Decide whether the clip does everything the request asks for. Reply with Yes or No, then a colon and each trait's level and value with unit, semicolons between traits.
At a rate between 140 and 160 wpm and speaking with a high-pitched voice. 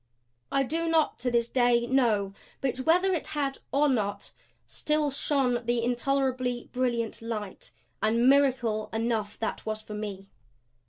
Yes: average, 145 wpm; high, 245 Hz